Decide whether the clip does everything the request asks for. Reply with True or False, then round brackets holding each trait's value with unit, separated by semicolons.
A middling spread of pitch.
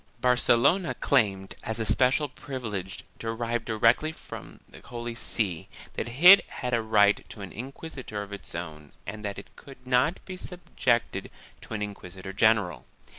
True (4.0 semitones)